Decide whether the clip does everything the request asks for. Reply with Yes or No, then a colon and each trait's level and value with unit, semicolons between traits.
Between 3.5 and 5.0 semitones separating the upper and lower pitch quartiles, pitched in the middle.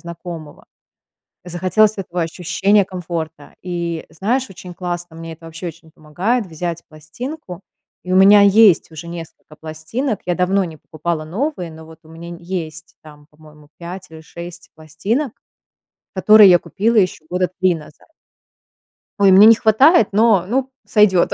Yes: average, 3.8 semitones; medium, 175 Hz